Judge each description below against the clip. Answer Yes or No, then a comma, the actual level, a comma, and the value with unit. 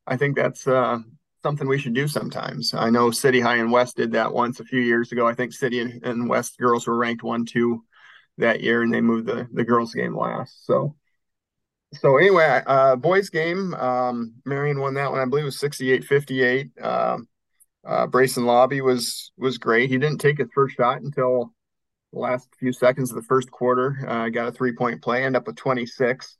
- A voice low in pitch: Yes, low, 125 Hz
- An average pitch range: No, narrow, 1.9 semitones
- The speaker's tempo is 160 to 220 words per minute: Yes, average, 200 wpm